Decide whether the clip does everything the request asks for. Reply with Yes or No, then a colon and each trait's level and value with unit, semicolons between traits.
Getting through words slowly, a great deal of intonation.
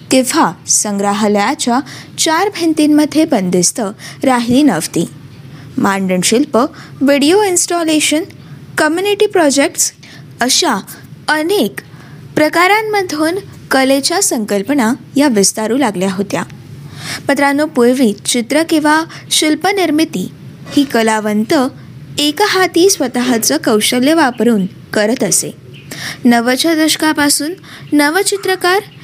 Yes: slow, 75 wpm; wide, 6.2 semitones